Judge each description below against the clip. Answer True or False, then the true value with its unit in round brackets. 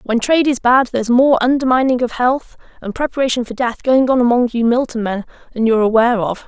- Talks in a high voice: True (245 Hz)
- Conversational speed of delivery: False (215 wpm)